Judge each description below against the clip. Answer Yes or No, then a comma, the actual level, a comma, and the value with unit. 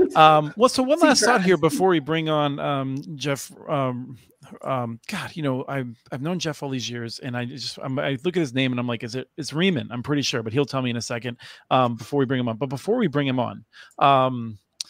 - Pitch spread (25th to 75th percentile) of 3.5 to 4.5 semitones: Yes, average, 4.1 semitones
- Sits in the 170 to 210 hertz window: No, low, 135 Hz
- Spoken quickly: Yes, fast, 260 wpm